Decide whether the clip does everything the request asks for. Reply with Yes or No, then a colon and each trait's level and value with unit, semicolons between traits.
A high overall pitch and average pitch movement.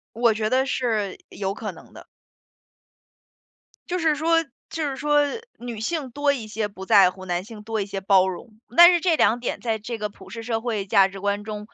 Yes: high, 220 Hz; average, 4.8 semitones